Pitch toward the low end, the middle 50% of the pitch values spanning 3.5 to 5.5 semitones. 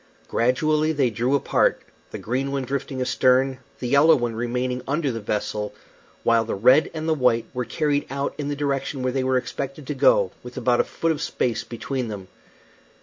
No: low, 130 Hz; average, 2.9 semitones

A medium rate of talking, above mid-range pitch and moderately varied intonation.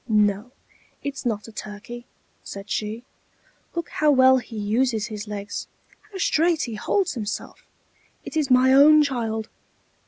Yes: average, 145 wpm; high, 240 Hz; average, 4.6 semitones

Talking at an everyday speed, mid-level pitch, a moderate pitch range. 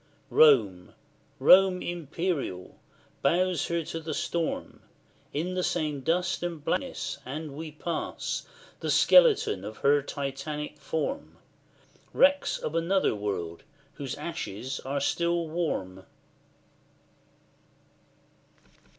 No: slow, 100 wpm; medium, 155 Hz; average, 4.0 semitones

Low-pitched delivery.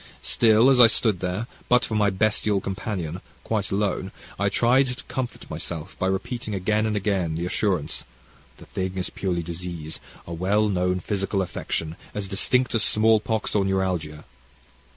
Yes: very low, 95 Hz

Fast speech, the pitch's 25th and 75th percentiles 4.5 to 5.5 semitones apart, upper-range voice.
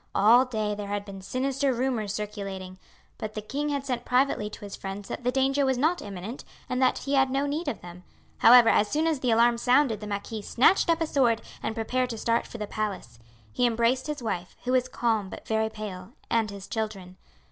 No: fast, 220 wpm; average, 4.0 semitones; high, 230 Hz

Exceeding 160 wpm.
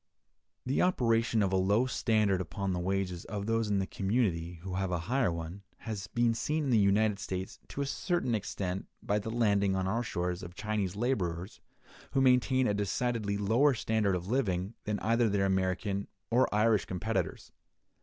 Yes: average, 180 wpm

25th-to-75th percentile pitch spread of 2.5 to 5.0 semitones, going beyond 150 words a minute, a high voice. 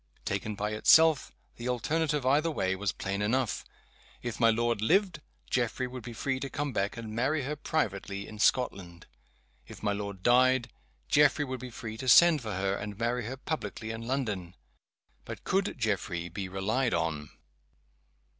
No: average, 4.6 semitones; average, 165 wpm; low, 115 Hz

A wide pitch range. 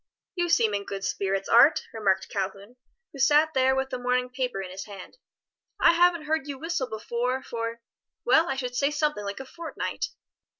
Yes: wide, 6.1 semitones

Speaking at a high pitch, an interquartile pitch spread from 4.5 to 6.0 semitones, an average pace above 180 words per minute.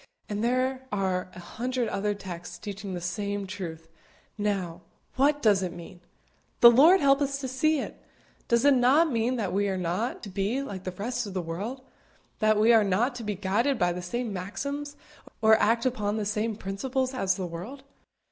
Yes: high, 210 Hz; average, 5.1 semitones; average, 195 wpm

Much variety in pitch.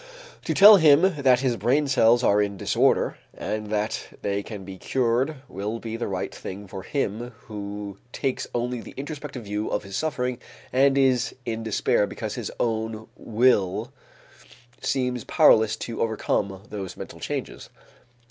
No: average, 3.9 semitones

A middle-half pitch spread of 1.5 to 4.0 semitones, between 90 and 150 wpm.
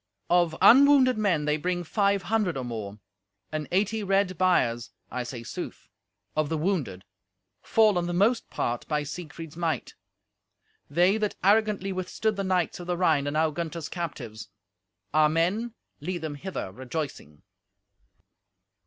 No: average, 4.8 semitones; average, 145 wpm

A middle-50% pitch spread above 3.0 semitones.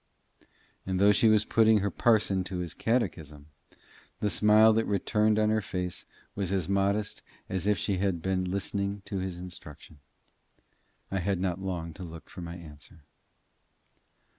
No: average, 2.7 semitones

